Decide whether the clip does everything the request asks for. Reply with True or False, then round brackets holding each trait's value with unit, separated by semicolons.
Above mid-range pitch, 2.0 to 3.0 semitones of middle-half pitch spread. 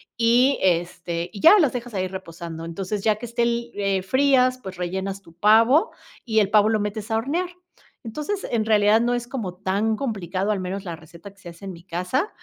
False (210 Hz; 4.3 semitones)